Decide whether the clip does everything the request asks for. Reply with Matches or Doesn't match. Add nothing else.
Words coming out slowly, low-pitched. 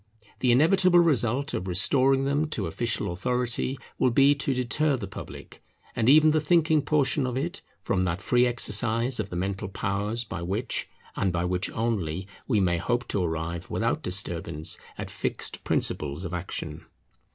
Doesn't match